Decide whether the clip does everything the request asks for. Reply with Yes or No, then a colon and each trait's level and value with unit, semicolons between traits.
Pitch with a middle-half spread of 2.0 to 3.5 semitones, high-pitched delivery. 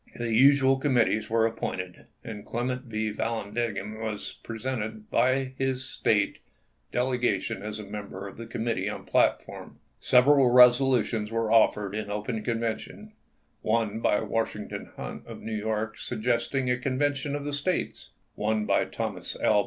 No: average, 3.1 semitones; low, 115 Hz